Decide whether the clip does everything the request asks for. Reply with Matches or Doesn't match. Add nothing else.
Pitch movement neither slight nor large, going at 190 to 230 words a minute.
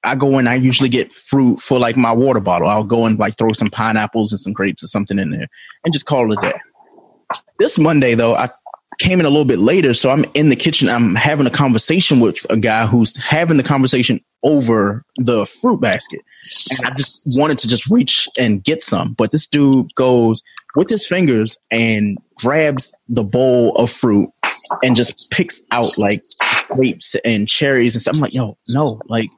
Matches